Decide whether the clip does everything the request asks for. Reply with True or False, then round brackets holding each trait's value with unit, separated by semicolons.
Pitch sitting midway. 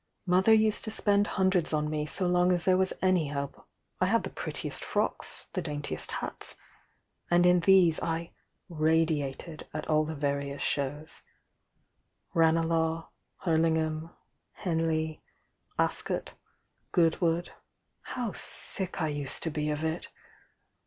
True (165 Hz)